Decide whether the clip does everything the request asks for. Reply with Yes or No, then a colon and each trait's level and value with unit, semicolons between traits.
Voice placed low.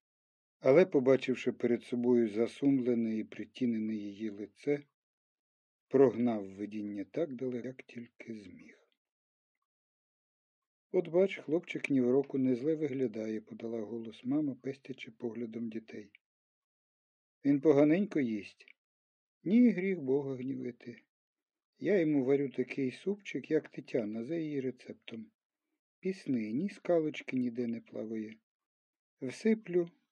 Yes: low, 130 Hz